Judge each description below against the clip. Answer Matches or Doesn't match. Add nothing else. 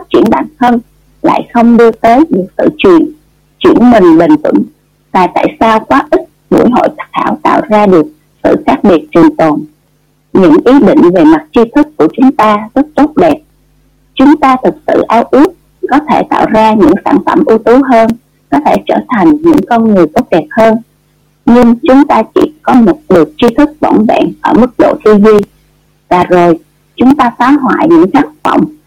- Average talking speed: Matches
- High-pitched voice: Matches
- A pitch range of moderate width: Doesn't match